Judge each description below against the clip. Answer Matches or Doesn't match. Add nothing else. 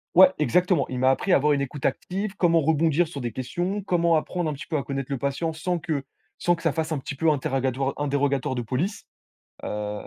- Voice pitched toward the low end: Doesn't match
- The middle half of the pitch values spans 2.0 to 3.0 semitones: Doesn't match